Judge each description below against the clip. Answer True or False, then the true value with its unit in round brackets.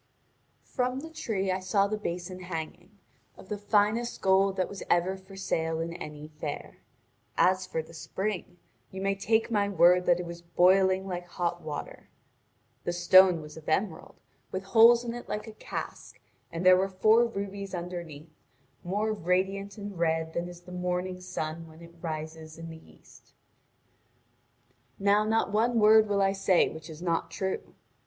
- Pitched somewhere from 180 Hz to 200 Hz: True (185 Hz)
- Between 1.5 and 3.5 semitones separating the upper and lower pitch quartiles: True (2.9 semitones)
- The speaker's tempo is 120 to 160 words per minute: False (170 wpm)